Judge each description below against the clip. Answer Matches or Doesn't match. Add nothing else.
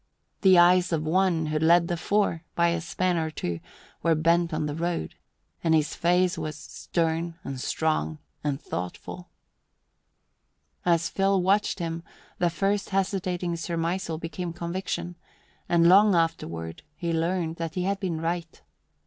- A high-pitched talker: Doesn't match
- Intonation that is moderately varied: Doesn't match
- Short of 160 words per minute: Matches